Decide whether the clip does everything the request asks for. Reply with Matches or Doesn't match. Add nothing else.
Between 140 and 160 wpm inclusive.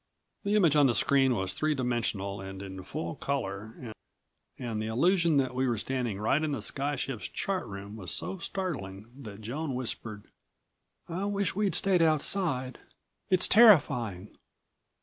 Matches